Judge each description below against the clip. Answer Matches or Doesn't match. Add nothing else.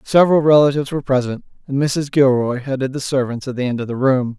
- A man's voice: Matches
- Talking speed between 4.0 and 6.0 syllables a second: Doesn't match